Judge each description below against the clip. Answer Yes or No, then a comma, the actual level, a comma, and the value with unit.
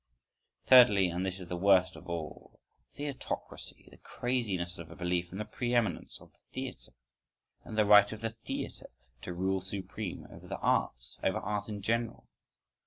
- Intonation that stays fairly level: No, average, 3.8 semitones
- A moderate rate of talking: Yes, average, 175 wpm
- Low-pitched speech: Yes, very low, 95 Hz